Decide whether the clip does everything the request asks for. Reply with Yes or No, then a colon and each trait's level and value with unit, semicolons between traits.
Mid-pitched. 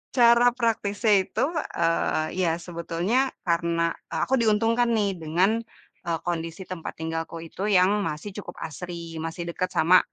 Yes: medium, 175 Hz